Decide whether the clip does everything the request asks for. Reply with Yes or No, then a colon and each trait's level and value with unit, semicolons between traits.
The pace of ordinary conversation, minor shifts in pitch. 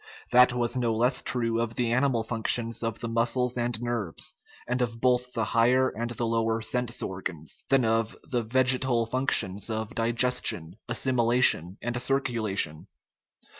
Yes: average, 150 wpm; narrow, 1.8 semitones